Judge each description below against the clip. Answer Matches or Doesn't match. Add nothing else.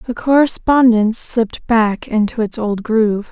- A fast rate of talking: Doesn't match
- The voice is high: Matches